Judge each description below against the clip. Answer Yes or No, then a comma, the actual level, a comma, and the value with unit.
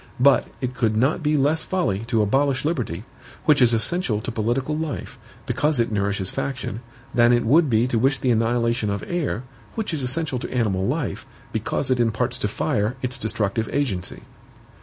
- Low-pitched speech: Yes, low, 120 Hz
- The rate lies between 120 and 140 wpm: No, average, 180 wpm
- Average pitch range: Yes, average, 4.1 semitones